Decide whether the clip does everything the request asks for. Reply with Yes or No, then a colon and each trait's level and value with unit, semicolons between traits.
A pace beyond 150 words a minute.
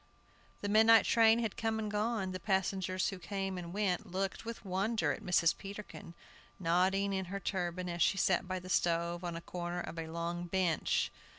Yes: average, 190 wpm